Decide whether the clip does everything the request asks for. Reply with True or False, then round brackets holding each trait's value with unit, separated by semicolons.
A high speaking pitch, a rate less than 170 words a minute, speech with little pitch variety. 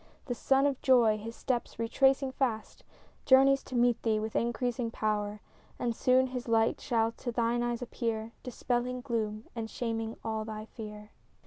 True (235 Hz; 160 wpm; 2.2 semitones)